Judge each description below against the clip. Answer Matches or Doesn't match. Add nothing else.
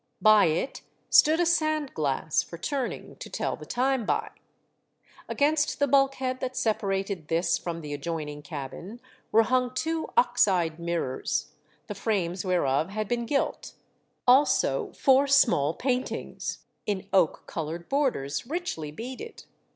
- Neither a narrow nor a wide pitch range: Doesn't match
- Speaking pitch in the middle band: Doesn't match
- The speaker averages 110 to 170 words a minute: Matches